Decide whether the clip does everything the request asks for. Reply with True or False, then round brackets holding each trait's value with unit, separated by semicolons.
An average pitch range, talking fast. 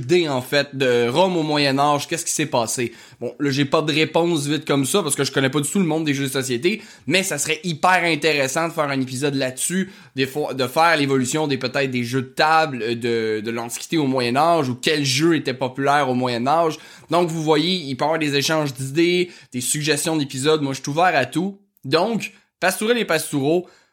True (3.8 semitones; 230 wpm)